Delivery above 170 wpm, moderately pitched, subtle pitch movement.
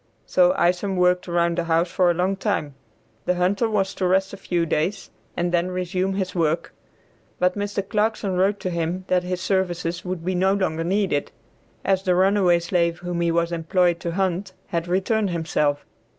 Yes: average, 185 wpm; medium, 180 Hz; narrow, 2.0 semitones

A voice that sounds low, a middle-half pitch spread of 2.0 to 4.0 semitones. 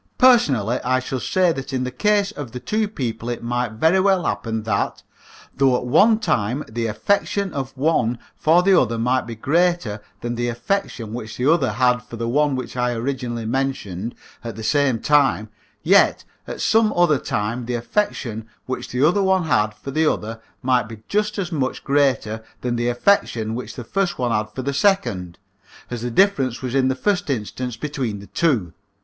No: low, 125 Hz; wide, 5.5 semitones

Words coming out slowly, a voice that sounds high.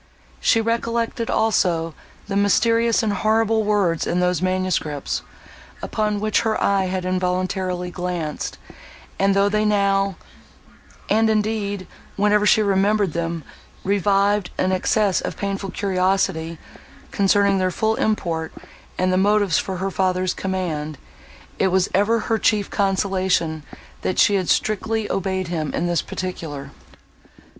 Yes: slow, 130 wpm; high, 195 Hz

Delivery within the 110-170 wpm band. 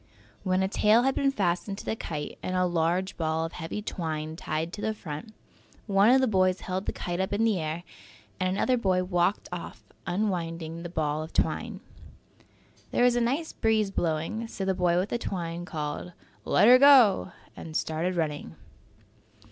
No: average, 185 wpm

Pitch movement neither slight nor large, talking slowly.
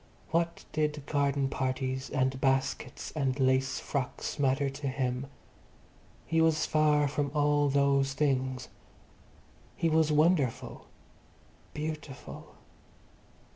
No: narrow, 2.3 semitones; slow, 100 wpm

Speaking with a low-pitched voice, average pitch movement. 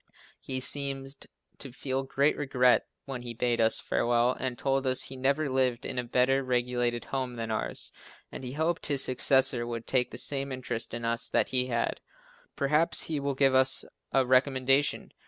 No: low, 130 Hz; narrow, 1.8 semitones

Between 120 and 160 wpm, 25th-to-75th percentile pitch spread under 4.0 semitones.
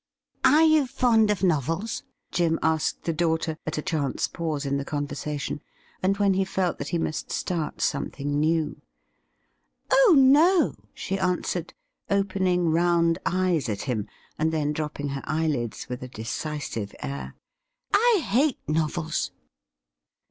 No: average, 150 wpm; average, 4.7 semitones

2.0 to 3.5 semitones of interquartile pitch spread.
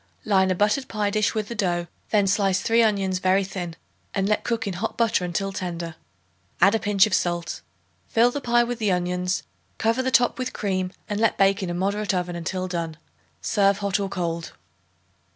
Yes: average, 2.9 semitones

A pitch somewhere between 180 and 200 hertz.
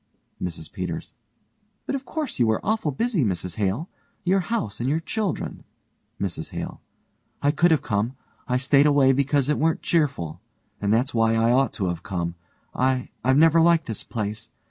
No: low, 130 Hz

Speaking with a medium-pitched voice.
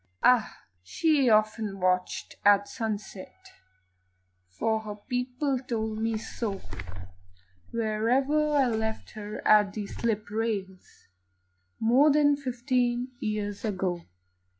No: high, 220 Hz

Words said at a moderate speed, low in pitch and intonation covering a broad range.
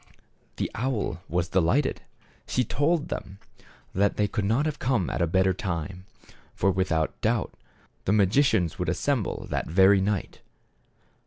Yes: average, 145 wpm; very low, 95 Hz; wide, 5.7 semitones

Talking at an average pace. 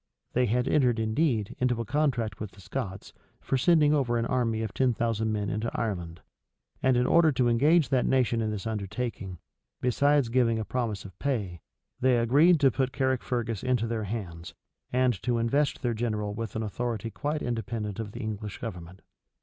Yes: average, 180 wpm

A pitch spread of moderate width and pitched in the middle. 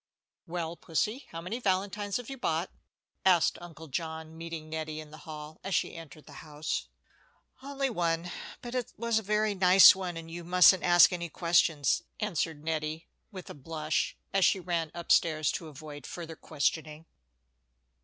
Yes: average, 3.2 semitones; medium, 165 Hz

